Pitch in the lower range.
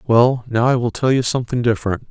Yes: low, 120 Hz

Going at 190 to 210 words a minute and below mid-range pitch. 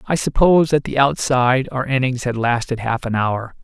Yes: average, 200 wpm; low, 130 Hz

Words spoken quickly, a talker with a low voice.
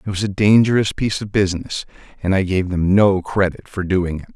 Yes: fast, 220 wpm; very low, 95 Hz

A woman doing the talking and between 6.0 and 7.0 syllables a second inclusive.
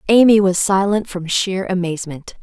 No: female; 4.9 syllables/s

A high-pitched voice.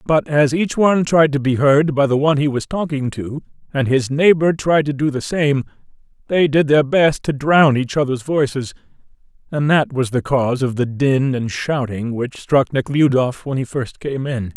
No: medium, 140 Hz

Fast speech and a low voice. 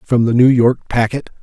Yes: fast, 210 wpm; low, 120 Hz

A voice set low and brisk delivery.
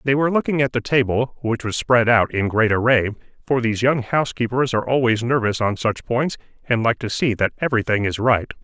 Yes: low, 120 Hz; fast, 215 wpm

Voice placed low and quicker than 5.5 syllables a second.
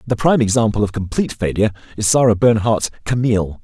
Yes: low, 110 Hz; 6.8 syllables/s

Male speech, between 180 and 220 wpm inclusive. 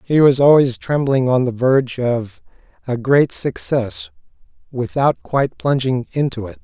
No: male; average, 145 wpm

